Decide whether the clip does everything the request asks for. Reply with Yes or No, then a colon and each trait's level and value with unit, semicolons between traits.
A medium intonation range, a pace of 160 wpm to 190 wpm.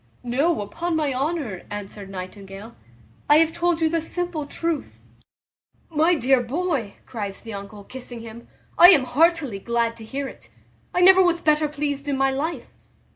No: wide, 6.3 semitones; average, 165 wpm